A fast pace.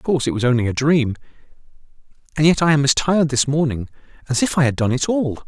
Yes: fast, 240 wpm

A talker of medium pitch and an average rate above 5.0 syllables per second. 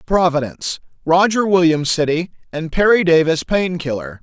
No: medium, 170 Hz; 4.9 syllables/s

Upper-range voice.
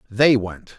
No: low, 115 Hz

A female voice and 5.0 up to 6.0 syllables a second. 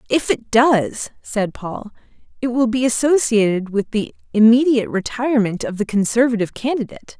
Yes: female; 5.4 syllables/s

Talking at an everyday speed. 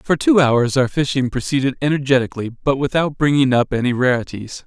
Yes: average, 165 wpm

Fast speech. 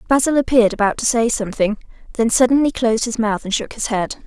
Yes: fast, 210 wpm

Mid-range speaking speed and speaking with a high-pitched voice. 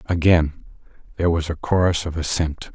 No: average, 155 wpm; very low, 80 Hz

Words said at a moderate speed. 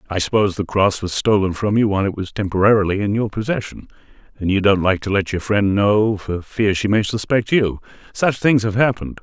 No: fast, 220 wpm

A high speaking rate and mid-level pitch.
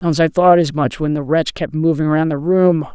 Yes: fast, 265 wpm; medium, 155 Hz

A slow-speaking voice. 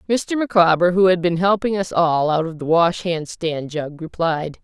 No: fast, 205 wpm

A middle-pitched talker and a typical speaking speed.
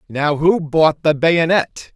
Yes: medium, 160 Hz; average, 155 wpm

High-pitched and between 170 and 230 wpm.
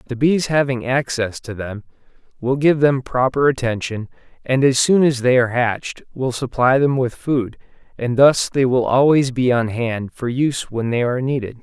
No: low, 125 Hz; average, 190 wpm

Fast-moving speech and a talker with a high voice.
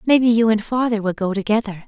Yes: fast, 255 wpm; high, 220 Hz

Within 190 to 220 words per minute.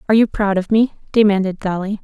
Yes: fast, 205 wpm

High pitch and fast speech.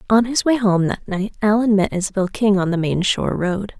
Yes: high, 200 Hz; fast, 235 wpm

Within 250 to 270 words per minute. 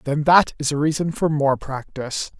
No: average, 200 wpm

